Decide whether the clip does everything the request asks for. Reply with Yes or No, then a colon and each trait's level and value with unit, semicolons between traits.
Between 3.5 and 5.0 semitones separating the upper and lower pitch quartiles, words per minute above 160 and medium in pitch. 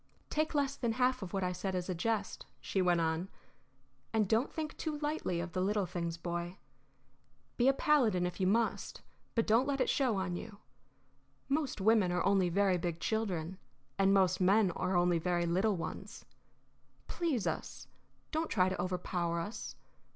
No: average, 4.4 semitones; average, 175 wpm; high, 195 Hz